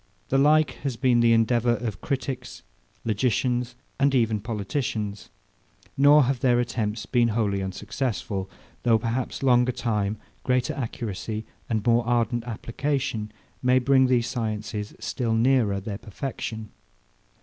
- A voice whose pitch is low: Yes, low, 120 Hz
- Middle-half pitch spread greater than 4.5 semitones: No, average, 2.8 semitones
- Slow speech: Yes, slow, 125 wpm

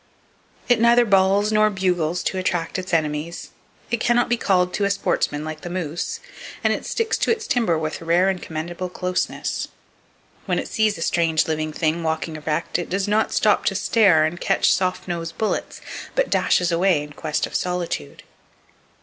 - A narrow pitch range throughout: No, average, 3.9 semitones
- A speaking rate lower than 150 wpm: No, average, 185 wpm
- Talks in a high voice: No, medium, 180 Hz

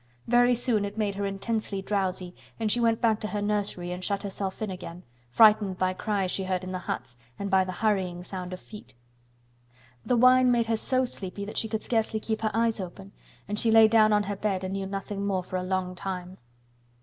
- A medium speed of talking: No, fast, 220 wpm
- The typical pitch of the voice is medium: No, high, 200 Hz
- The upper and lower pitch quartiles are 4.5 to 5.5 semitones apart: No, average, 2.9 semitones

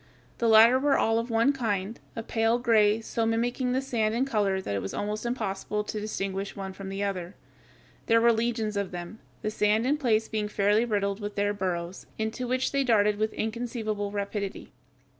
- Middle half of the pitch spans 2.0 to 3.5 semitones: Yes, narrow, 2.5 semitones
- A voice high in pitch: Yes, high, 215 Hz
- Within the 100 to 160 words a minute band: No, average, 195 wpm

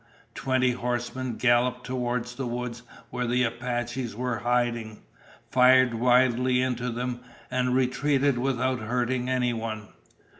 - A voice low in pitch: Yes, low, 125 Hz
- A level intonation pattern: Yes, narrow, 1.0 semitones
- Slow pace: Yes, slow, 115 wpm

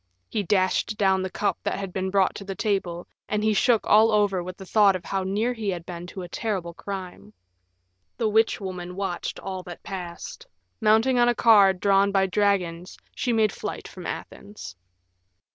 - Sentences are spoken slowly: No, average, 190 wpm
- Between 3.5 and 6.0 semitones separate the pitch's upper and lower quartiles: No, average, 2.7 semitones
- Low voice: No, high, 195 Hz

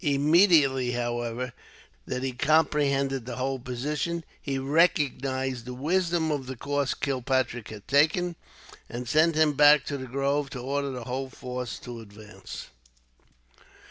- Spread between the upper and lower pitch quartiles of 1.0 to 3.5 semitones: Yes, average, 2.9 semitones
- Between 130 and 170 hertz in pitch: Yes, low, 135 Hz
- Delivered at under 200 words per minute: Yes, average, 140 wpm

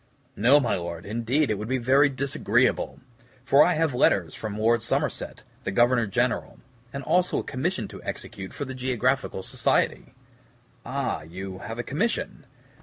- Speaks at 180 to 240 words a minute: No, average, 160 wpm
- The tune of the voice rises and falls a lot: No, average, 4.5 semitones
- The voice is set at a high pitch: No, low, 125 Hz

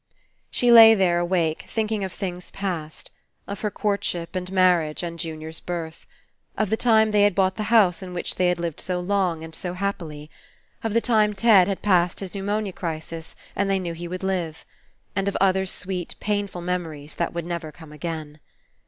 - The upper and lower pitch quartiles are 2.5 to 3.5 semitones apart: Yes, average, 3.1 semitones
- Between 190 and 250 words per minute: Yes, average, 200 wpm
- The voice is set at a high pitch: No, medium, 180 Hz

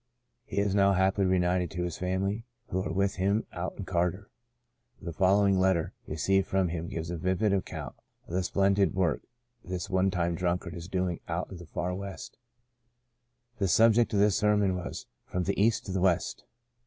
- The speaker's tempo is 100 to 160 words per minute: No, average, 190 wpm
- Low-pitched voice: Yes, very low, 95 Hz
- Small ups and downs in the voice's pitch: Yes, narrow, 1.9 semitones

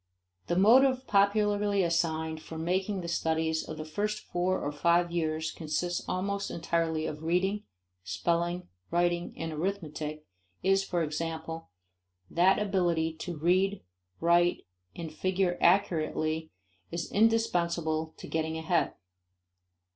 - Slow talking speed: Yes, slow, 120 wpm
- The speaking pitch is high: No, medium, 170 Hz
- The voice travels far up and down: No, average, 3.0 semitones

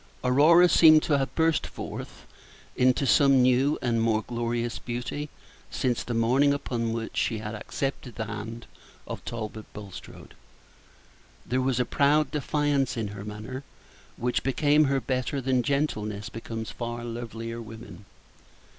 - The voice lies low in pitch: Yes, low, 125 Hz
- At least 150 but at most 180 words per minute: No, average, 140 wpm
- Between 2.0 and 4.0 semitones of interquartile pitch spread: Yes, average, 3.4 semitones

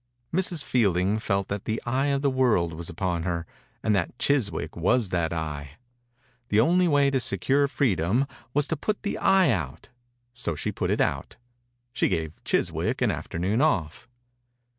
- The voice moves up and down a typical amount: No, wide, 8.3 semitones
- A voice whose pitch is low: Yes, low, 105 Hz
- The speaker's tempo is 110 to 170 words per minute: Yes, average, 165 wpm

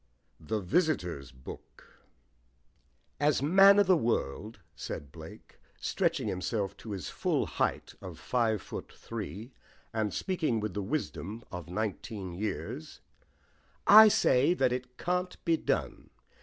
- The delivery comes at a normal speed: No, slow, 130 wpm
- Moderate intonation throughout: No, wide, 8.5 semitones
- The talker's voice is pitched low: Yes, low, 110 Hz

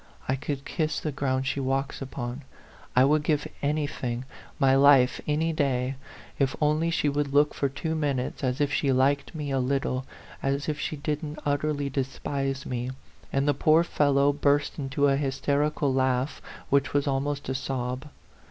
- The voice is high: No, medium, 140 Hz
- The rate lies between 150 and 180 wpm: Yes, average, 170 wpm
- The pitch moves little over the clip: Yes, narrow, 1.7 semitones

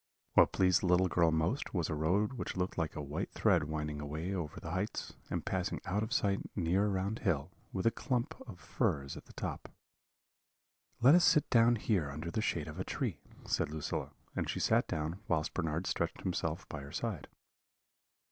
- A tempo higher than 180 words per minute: Yes, average, 195 wpm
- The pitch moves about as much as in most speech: Yes, average, 4.7 semitones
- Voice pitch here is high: No, very low, 90 Hz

